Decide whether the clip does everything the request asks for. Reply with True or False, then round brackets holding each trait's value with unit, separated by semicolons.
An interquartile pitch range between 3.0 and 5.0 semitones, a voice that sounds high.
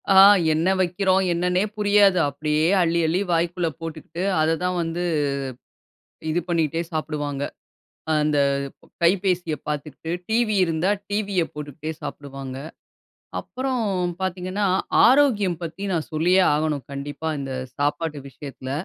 False (3.5 semitones; 165 Hz)